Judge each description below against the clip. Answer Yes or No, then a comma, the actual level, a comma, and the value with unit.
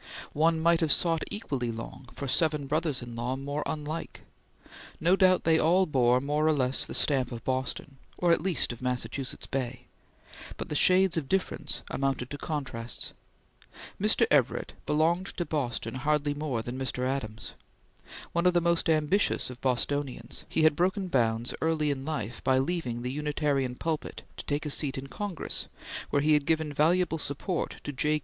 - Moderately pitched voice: Yes, medium, 145 Hz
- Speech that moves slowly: No, average, 175 wpm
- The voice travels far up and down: No, average, 3.8 semitones